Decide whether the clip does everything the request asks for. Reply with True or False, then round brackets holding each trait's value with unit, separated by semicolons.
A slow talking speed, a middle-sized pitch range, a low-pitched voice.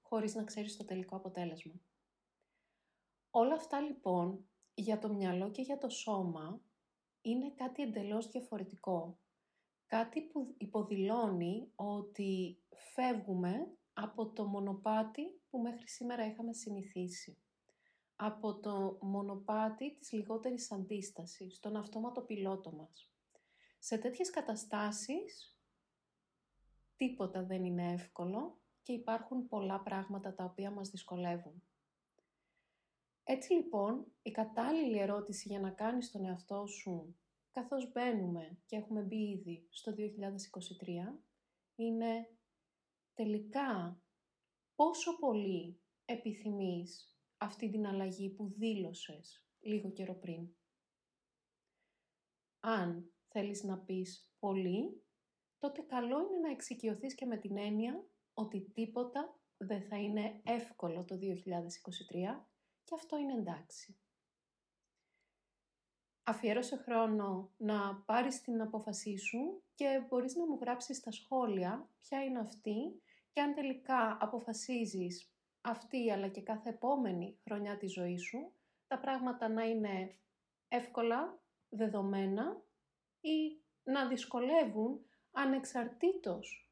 False (110 wpm; 4.3 semitones; 215 Hz)